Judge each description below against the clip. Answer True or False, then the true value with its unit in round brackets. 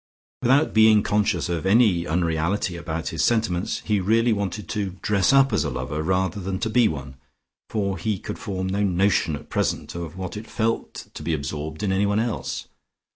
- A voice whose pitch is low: True (95 Hz)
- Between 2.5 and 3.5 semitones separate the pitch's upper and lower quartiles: False (4.0 semitones)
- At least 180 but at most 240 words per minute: True (185 wpm)